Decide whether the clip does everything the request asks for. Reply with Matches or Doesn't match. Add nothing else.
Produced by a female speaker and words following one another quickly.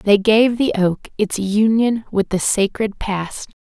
Doesn't match